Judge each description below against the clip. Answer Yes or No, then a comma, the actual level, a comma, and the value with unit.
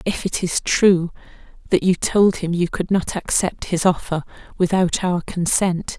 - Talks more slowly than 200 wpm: Yes, average, 170 wpm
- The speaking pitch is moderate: Yes, medium, 180 Hz